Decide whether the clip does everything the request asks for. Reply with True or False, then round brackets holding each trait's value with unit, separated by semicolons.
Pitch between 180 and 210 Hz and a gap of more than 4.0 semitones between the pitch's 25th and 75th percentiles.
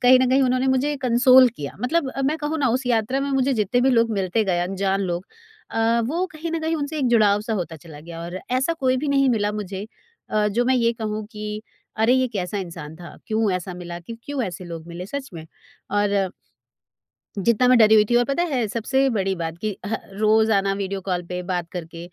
False (220 Hz; 5.5 semitones)